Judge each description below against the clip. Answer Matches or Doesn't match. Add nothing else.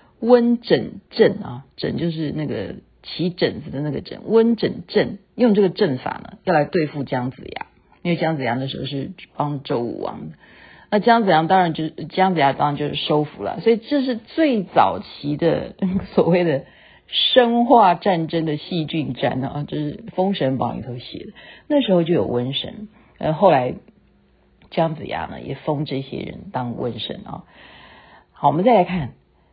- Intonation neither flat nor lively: Doesn't match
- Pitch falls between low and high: Matches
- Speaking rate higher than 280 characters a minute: Doesn't match